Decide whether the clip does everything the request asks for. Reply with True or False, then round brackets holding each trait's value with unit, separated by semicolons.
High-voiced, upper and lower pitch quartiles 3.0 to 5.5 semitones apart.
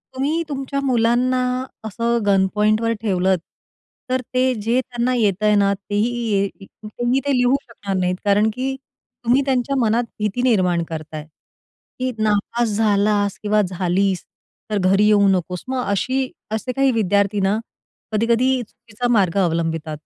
True (215 Hz; 3.9 semitones)